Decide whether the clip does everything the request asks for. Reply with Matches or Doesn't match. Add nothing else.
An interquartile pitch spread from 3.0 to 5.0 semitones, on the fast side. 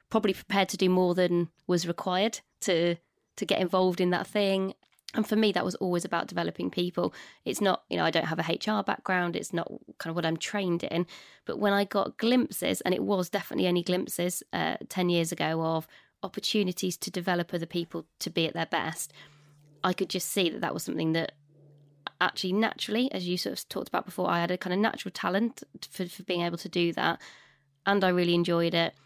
Doesn't match